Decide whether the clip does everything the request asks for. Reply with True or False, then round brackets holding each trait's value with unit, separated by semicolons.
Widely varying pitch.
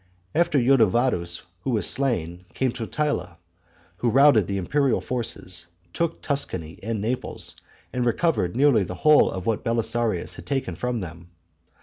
True (6.5 semitones)